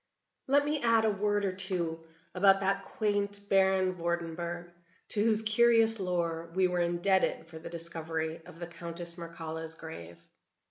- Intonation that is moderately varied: Yes, average, 3.3 semitones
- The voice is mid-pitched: Yes, medium, 180 Hz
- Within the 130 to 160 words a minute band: Yes, average, 150 wpm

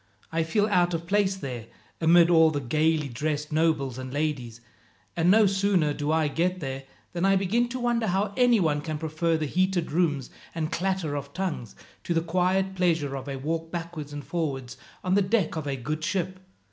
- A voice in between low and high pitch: Yes, medium, 165 Hz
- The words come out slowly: No, average, 195 wpm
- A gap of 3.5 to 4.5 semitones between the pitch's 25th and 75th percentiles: Yes, average, 4.1 semitones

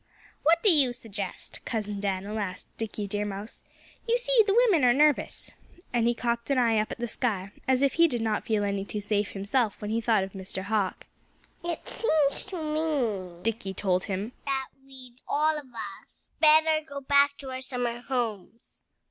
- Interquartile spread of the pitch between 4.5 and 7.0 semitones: Yes, wide, 5.4 semitones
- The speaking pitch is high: Yes, high, 235 Hz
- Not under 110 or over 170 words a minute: No, average, 190 wpm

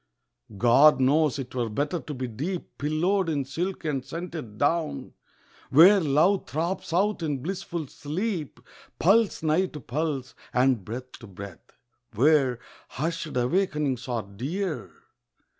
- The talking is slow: Yes, slow, 125 wpm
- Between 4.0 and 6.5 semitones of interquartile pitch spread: Yes, average, 5.0 semitones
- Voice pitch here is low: No, medium, 150 Hz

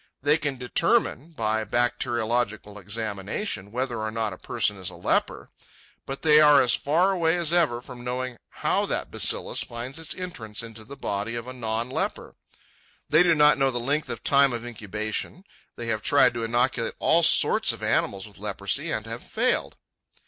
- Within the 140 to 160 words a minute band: No, average, 180 wpm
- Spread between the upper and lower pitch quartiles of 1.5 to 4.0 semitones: No, average, 4.8 semitones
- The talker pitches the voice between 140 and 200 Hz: No, low, 120 Hz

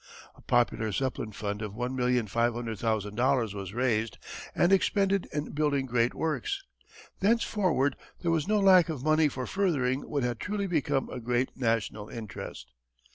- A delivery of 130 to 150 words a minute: Yes, average, 140 wpm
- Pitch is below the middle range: Yes, low, 130 Hz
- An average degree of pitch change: No, wide, 5.9 semitones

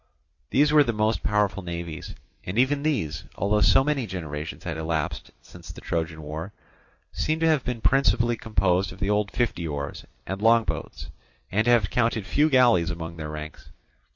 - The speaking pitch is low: Yes, low, 100 Hz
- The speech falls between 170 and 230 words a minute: Yes, average, 180 wpm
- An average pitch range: No, wide, 6.3 semitones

